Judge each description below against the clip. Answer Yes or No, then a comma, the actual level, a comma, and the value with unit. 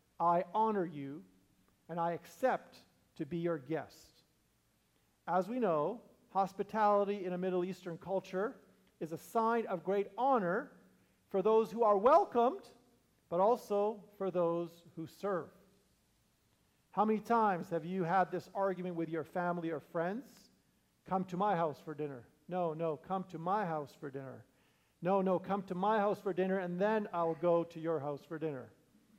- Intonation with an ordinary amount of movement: Yes, average, 3.9 semitones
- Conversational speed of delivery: Yes, average, 165 wpm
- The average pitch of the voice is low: No, medium, 180 Hz